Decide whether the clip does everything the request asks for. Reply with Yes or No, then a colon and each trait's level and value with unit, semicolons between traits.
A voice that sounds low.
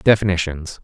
Yes: very low, 90 Hz